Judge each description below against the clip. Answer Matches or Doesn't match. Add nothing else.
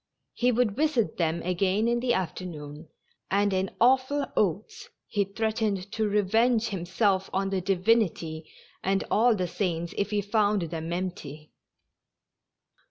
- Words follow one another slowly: Doesn't match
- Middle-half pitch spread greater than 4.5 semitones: Doesn't match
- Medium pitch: Doesn't match